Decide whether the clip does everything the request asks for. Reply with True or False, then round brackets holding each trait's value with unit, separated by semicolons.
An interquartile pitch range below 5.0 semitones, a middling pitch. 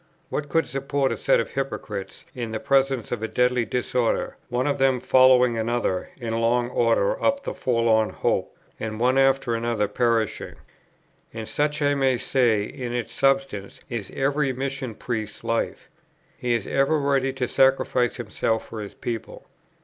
False (2.9 semitones; 125 Hz)